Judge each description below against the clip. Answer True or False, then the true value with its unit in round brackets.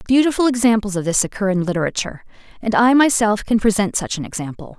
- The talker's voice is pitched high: True (210 Hz)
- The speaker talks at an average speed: True (190 wpm)